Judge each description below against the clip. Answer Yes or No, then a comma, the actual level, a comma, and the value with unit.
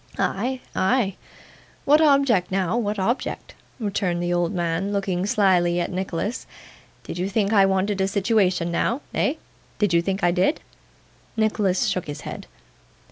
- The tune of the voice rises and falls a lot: No, average, 3.3 semitones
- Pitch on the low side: No, high, 195 Hz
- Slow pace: No, average, 150 wpm